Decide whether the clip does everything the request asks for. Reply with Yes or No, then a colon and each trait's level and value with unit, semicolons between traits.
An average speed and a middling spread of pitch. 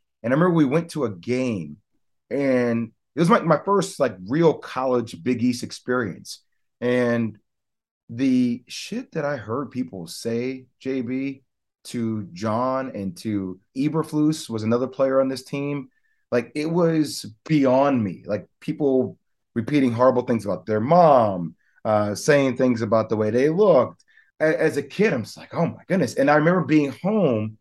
Yes: average, 165 wpm; average, 4.5 semitones